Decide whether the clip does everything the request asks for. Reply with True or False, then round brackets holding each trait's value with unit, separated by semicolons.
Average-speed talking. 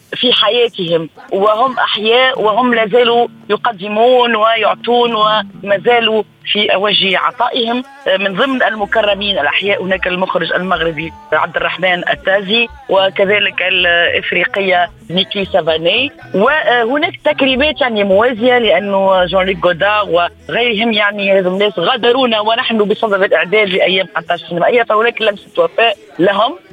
True (110 wpm)